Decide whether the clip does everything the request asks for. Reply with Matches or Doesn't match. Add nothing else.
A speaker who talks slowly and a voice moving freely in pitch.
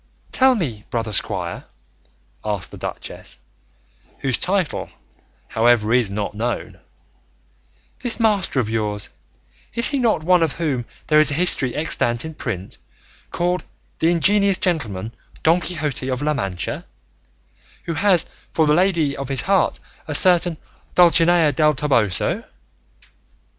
Matches